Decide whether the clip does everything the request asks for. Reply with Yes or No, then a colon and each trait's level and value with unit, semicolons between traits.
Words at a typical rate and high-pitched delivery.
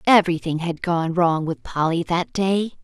No: average, 170 wpm; medium, 170 Hz